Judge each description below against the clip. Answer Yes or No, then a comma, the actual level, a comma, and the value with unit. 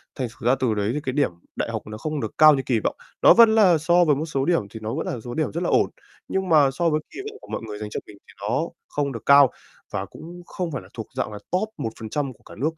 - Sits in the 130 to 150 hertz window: Yes, medium, 140 Hz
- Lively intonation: Yes, wide, 6.1 semitones